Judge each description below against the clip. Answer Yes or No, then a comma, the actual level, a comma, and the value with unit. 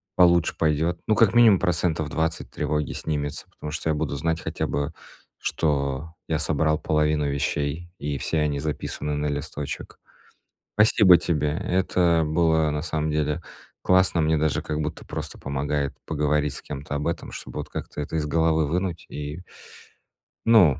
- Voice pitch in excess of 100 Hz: No, very low, 75 Hz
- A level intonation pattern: Yes, narrow, 2.2 semitones